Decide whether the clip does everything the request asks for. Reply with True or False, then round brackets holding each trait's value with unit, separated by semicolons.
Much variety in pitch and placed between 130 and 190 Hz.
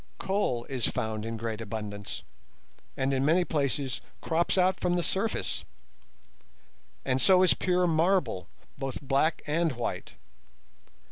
True (7.1 semitones; 140 Hz)